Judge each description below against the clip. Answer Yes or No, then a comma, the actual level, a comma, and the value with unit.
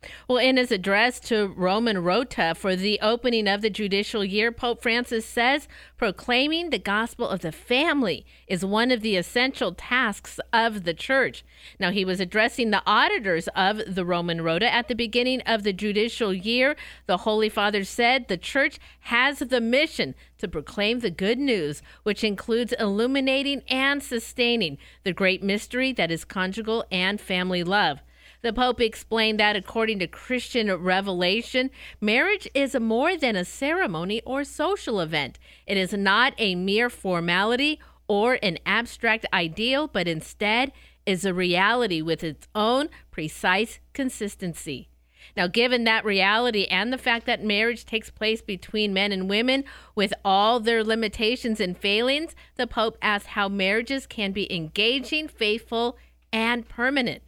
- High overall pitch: Yes, high, 220 Hz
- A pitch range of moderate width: Yes, average, 4.0 semitones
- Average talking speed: Yes, average, 155 wpm